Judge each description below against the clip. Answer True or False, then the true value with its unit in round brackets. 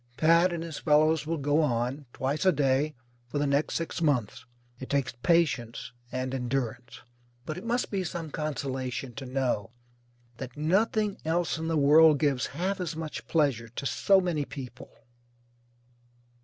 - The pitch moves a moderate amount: True (3.9 semitones)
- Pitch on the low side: False (150 Hz)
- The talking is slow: False (155 wpm)